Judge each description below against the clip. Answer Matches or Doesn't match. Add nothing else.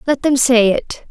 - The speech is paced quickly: Matches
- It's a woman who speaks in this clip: Matches